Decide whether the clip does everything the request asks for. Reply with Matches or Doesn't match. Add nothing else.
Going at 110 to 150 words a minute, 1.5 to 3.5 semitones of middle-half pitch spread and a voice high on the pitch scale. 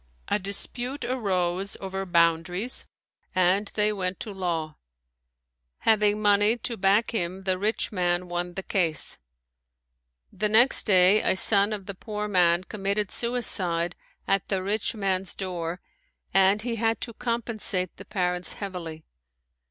Matches